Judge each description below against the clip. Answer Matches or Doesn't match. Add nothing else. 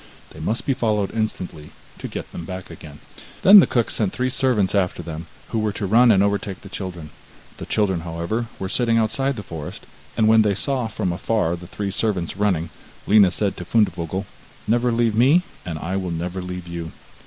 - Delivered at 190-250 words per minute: Matches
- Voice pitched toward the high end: Doesn't match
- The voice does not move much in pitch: Doesn't match